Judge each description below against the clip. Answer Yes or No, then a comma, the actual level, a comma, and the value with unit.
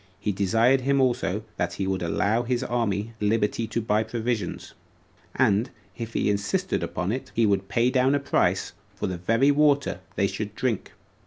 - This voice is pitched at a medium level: No, low, 115 Hz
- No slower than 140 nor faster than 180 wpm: Yes, average, 175 wpm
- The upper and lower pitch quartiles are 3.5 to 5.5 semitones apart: Yes, average, 3.9 semitones